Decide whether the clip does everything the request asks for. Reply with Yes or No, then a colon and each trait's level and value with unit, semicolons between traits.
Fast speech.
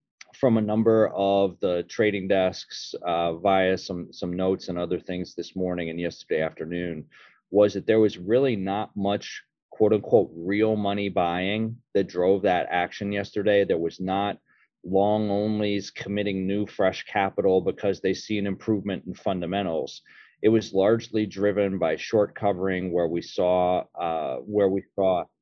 No: average, 160 wpm